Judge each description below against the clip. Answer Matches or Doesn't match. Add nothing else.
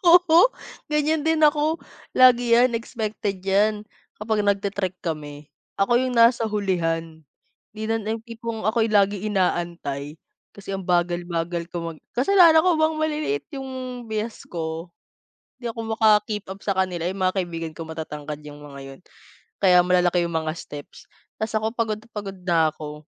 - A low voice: Doesn't match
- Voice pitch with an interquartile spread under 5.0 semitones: Doesn't match